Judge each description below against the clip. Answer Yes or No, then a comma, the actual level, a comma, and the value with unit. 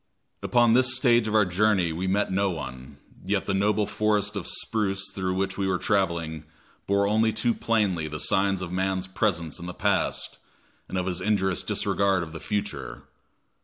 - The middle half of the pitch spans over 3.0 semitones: No, average, 2.7 semitones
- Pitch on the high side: No, very low, 95 Hz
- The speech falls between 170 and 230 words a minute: Yes, average, 180 wpm